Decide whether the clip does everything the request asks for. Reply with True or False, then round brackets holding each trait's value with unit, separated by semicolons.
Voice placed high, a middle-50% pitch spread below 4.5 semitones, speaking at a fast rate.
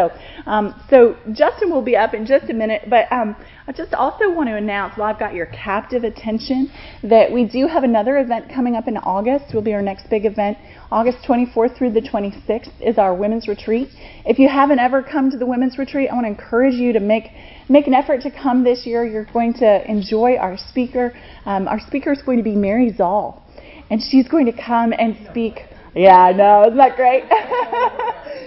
True (235 Hz; 3.7 semitones; 210 wpm)